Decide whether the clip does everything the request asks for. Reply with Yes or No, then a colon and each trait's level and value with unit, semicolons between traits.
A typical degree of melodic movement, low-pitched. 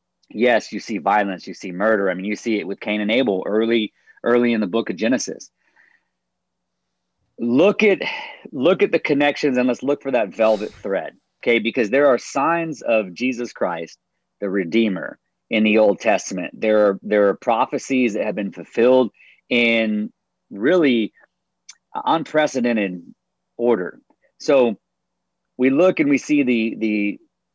Yes: average, 3.6 semitones; low, 115 Hz